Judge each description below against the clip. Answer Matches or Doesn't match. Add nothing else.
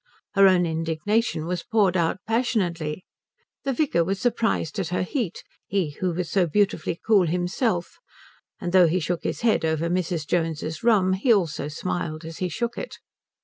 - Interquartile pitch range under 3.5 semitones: Doesn't match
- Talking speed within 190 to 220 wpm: Doesn't match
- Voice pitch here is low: Doesn't match